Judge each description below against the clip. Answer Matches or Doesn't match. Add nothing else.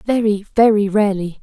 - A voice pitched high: Matches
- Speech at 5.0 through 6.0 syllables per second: Matches